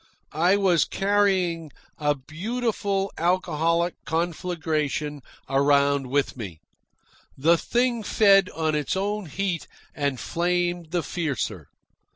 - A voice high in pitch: No, medium, 170 Hz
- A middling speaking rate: No, slow, 105 wpm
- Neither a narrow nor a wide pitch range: Yes, average, 4.7 semitones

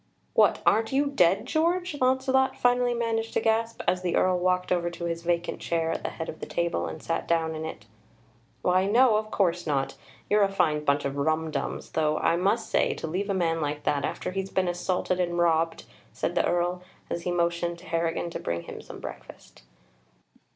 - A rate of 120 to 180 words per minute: No, fast, 205 wpm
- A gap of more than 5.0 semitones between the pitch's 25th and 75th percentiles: No, average, 4.1 semitones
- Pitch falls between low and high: Yes, medium, 175 Hz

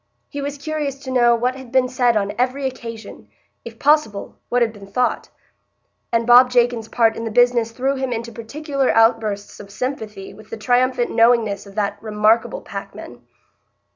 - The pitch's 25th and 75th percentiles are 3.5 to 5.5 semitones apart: No, narrow, 2.5 semitones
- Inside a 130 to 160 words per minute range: No, average, 170 wpm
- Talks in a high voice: Yes, high, 240 Hz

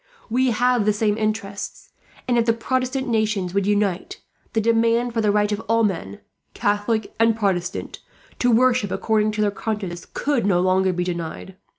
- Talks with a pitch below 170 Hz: No, high, 215 Hz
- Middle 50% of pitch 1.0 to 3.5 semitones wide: Yes, average, 2.7 semitones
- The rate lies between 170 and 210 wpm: Yes, average, 175 wpm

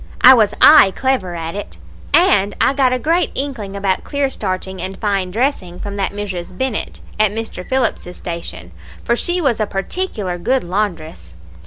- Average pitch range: No, wide, 5.9 semitones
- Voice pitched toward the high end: Yes, high, 205 Hz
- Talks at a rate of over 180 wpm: No, average, 170 wpm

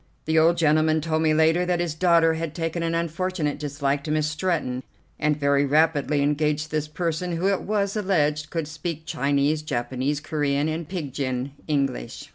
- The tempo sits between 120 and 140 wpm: No, average, 175 wpm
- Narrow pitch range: Yes, narrow, 2.3 semitones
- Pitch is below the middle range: No, medium, 155 Hz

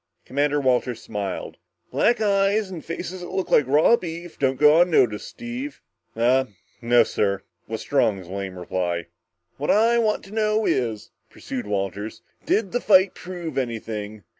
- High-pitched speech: No, medium, 140 Hz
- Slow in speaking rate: No, average, 150 wpm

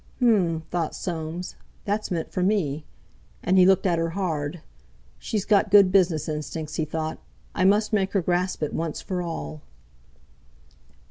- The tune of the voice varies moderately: Yes, average, 3.4 semitones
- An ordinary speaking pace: Yes, average, 155 wpm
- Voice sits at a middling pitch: Yes, medium, 175 Hz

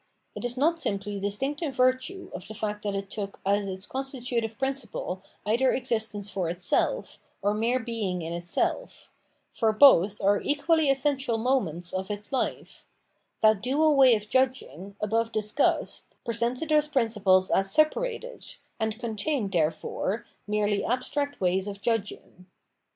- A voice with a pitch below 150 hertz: No, high, 225 Hz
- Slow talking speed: No, average, 145 wpm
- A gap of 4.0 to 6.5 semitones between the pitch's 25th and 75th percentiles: Yes, average, 5.0 semitones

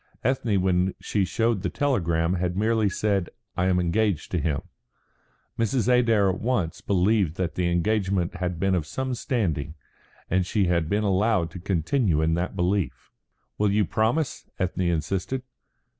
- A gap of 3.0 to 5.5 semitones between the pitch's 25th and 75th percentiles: Yes, average, 3.9 semitones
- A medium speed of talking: Yes, average, 160 wpm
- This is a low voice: Yes, very low, 95 Hz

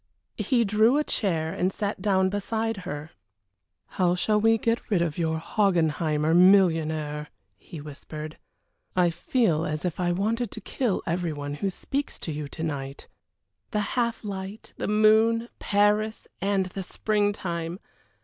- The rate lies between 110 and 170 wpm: Yes, average, 150 wpm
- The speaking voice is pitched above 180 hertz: Yes, high, 190 Hz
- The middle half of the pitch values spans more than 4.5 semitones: Yes, average, 4.9 semitones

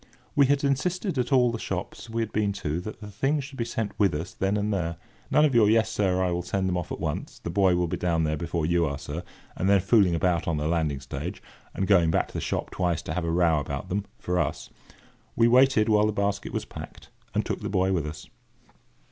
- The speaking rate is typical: No, fast, 250 wpm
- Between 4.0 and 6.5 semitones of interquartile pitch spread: Yes, average, 4.6 semitones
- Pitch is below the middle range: Yes, very low, 95 Hz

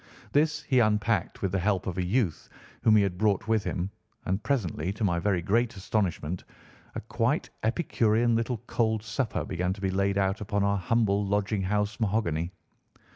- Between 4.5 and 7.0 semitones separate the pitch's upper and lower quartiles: No, average, 2.9 semitones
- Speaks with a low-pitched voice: Yes, low, 100 Hz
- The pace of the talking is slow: No, average, 180 wpm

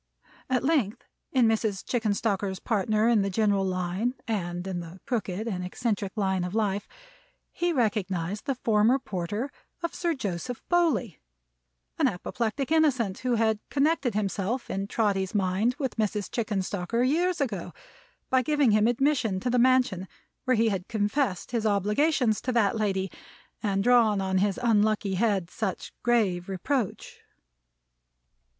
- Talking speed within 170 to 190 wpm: No, average, 145 wpm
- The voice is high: Yes, high, 215 Hz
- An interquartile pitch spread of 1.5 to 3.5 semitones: No, average, 4.3 semitones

